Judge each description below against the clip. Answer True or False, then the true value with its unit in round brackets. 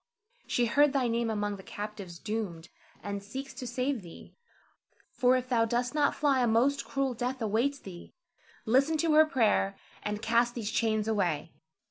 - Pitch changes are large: False (4.1 semitones)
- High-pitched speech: True (235 Hz)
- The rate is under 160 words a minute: False (170 wpm)